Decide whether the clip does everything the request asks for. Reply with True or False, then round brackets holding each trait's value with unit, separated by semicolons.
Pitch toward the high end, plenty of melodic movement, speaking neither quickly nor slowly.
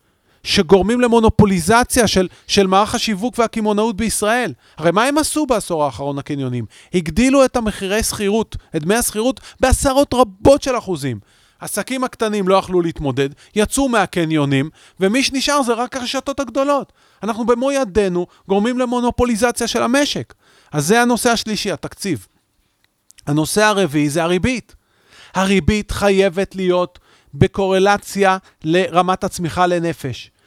True (200 Hz; 6.0 semitones; 120 wpm)